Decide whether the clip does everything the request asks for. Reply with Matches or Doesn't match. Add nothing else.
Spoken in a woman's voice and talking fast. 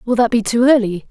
Matches